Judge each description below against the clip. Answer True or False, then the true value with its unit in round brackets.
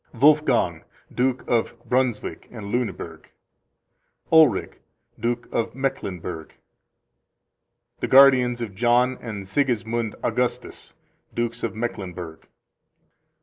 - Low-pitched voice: True (120 Hz)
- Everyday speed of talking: False (90 wpm)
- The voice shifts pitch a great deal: False (3.4 semitones)